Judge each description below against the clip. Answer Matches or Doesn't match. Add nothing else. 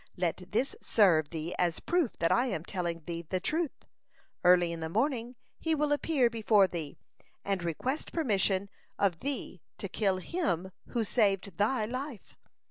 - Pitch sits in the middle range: Doesn't match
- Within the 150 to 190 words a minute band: Matches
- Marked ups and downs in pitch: Matches